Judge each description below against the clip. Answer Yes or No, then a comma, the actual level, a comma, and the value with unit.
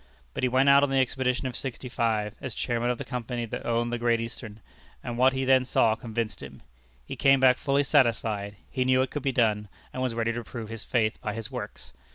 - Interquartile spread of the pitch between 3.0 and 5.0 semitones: No, narrow, 2.4 semitones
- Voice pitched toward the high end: No, low, 120 Hz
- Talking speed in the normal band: No, fast, 230 wpm